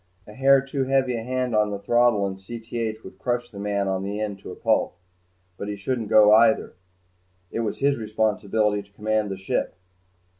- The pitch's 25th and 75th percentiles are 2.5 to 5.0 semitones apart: Yes, average, 2.9 semitones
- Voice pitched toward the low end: Yes, low, 110 Hz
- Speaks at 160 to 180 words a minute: No, average, 195 wpm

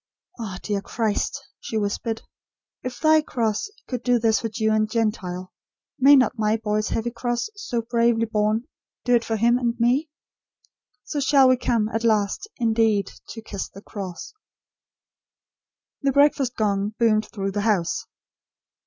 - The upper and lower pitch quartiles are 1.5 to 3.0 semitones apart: Yes, narrow, 2.5 semitones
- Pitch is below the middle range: No, high, 225 Hz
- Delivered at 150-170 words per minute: Yes, average, 155 wpm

